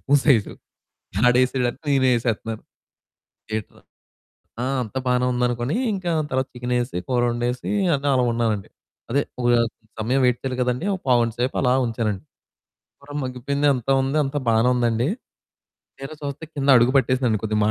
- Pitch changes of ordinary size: No, narrow, 2.2 semitones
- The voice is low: Yes, low, 125 Hz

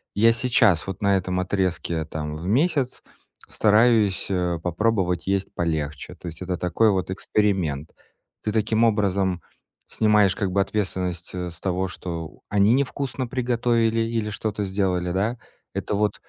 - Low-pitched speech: Yes, low, 100 Hz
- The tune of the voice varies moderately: Yes, average, 3.8 semitones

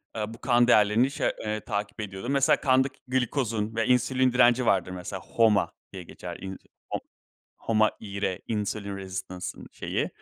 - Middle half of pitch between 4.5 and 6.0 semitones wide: No, average, 3.8 semitones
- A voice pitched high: No, low, 110 Hz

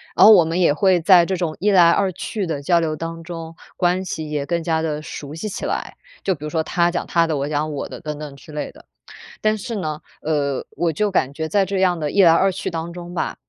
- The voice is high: No, medium, 165 Hz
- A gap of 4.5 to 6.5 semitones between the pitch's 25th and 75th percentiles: No, average, 3.0 semitones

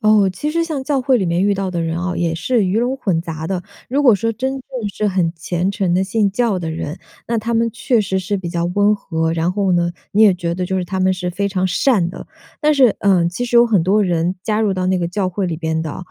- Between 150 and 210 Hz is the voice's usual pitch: Yes, high, 190 Hz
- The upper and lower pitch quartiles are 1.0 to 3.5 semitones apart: No, average, 4.1 semitones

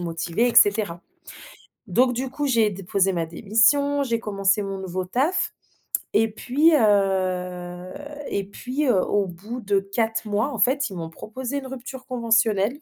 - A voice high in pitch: Yes, high, 210 Hz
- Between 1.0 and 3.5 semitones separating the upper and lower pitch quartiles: No, average, 4.8 semitones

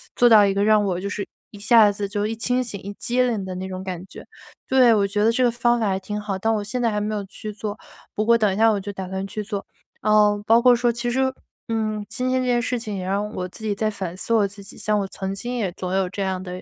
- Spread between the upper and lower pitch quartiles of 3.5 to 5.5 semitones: No, average, 2.8 semitones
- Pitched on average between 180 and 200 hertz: No, high, 210 Hz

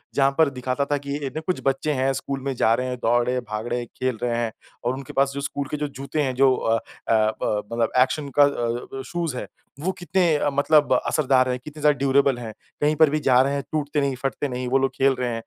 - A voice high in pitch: No, low, 135 Hz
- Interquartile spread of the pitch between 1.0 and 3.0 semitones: Yes, narrow, 2.4 semitones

